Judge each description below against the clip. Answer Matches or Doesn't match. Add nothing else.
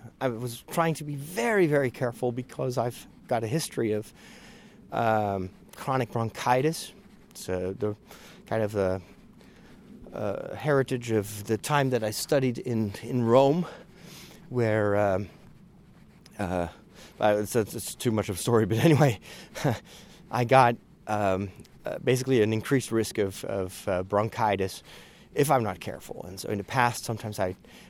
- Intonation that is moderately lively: Matches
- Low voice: Matches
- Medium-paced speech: Matches